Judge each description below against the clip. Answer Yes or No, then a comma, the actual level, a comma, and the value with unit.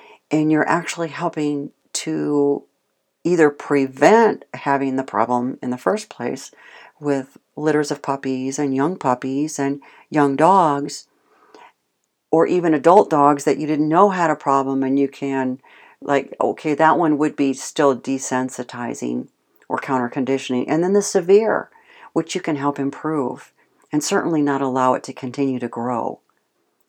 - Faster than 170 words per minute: No, average, 150 wpm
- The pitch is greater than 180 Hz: No, medium, 140 Hz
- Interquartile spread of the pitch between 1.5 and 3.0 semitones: Yes, average, 2.7 semitones